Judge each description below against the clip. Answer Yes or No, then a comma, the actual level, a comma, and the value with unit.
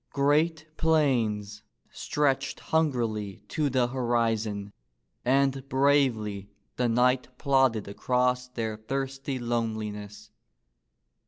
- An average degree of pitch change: Yes, average, 4.0 semitones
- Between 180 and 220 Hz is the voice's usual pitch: No, low, 125 Hz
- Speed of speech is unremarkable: No, slow, 85 wpm